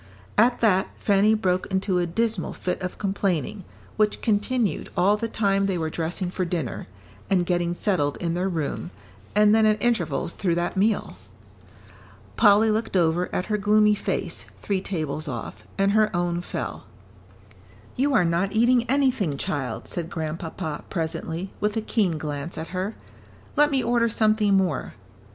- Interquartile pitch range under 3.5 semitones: No, average, 4.0 semitones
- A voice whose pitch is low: No, high, 190 Hz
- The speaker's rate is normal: Yes, average, 160 wpm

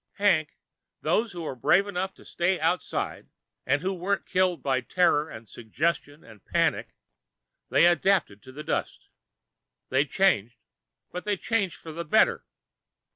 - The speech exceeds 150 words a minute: No, average, 145 wpm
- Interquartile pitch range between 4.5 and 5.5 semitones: Yes, average, 5.1 semitones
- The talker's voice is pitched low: No, medium, 170 Hz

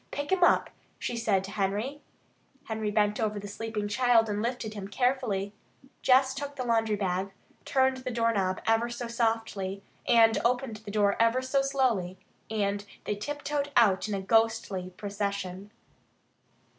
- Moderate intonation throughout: Yes, average, 3.6 semitones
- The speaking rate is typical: Yes, average, 150 wpm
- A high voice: Yes, high, 220 Hz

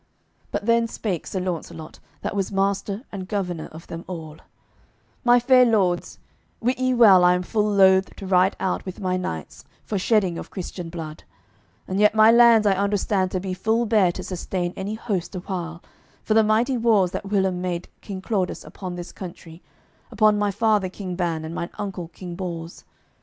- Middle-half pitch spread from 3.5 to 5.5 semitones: No, average, 3.1 semitones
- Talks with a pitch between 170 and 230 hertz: Yes, high, 190 Hz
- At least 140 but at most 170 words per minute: No, average, 190 wpm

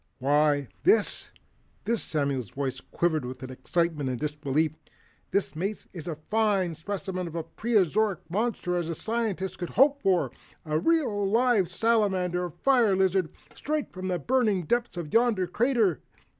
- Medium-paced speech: Yes, average, 155 wpm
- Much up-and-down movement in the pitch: Yes, wide, 5.9 semitones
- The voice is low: No, medium, 185 Hz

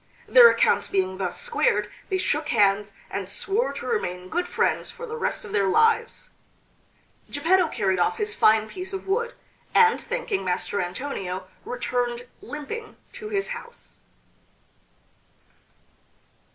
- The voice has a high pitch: Yes, very high, 295 Hz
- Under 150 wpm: Yes, slow, 135 wpm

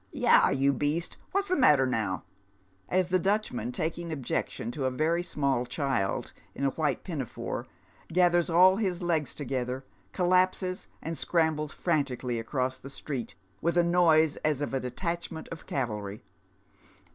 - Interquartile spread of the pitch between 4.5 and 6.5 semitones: Yes, average, 4.9 semitones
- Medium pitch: Yes, medium, 155 Hz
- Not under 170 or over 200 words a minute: No, average, 150 wpm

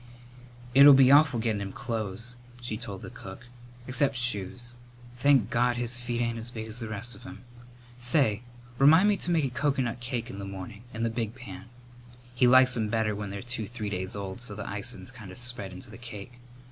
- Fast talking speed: Yes, fast, 210 wpm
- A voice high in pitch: No, low, 120 Hz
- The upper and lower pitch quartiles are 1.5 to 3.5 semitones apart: Yes, average, 3.0 semitones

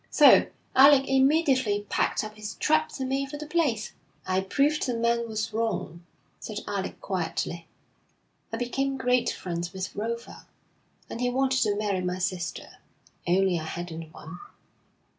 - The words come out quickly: No, average, 150 wpm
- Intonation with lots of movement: Yes, wide, 6.0 semitones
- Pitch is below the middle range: No, high, 225 Hz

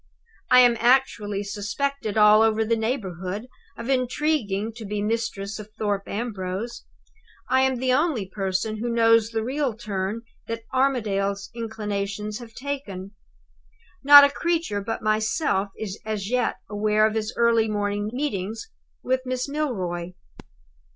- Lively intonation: No, average, 3.5 semitones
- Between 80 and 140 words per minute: Yes, slow, 135 wpm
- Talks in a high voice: Yes, high, 220 Hz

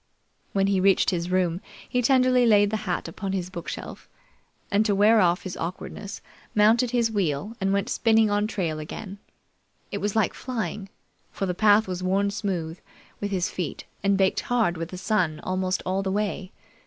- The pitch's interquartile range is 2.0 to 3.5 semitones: Yes, average, 2.7 semitones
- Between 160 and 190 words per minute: Yes, average, 180 wpm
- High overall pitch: Yes, high, 195 Hz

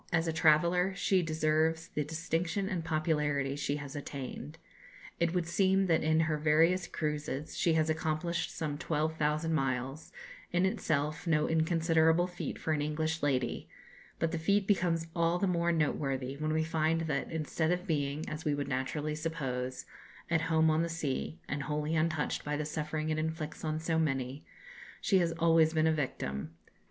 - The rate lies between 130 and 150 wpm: No, average, 170 wpm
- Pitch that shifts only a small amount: Yes, narrow, 1.7 semitones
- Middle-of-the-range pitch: Yes, medium, 160 Hz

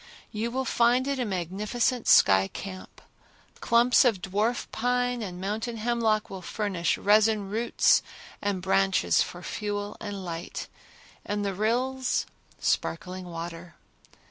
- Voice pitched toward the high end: Yes, high, 210 Hz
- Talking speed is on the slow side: Yes, slow, 125 wpm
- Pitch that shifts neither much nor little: Yes, average, 4.1 semitones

